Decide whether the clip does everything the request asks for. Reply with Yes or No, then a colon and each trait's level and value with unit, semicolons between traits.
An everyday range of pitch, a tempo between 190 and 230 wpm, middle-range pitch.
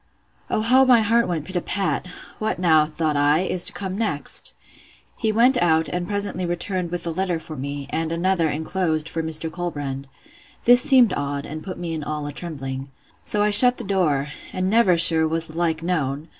Yes: average, 3.7 semitones; average, 200 wpm; medium, 170 Hz